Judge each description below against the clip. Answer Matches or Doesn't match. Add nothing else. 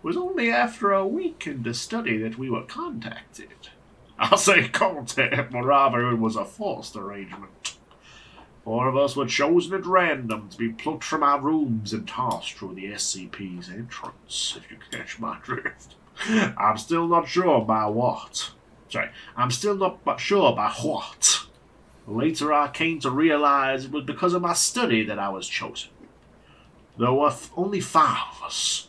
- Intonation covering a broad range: Matches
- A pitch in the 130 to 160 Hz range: Matches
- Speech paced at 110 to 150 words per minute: Doesn't match